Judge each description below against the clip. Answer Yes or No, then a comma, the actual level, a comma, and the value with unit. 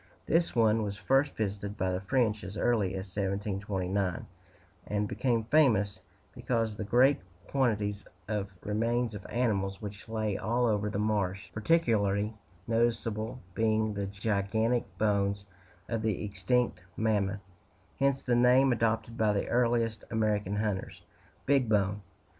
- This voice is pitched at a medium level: No, low, 110 Hz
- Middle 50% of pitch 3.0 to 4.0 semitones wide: No, narrow, 2.5 semitones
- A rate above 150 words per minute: No, slow, 135 wpm